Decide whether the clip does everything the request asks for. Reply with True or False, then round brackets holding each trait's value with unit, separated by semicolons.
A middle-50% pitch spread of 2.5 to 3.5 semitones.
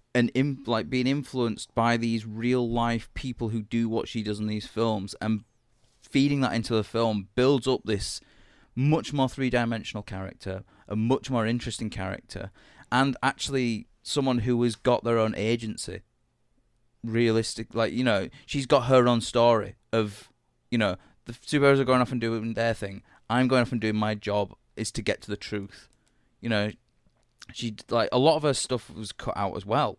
True (2.8 semitones)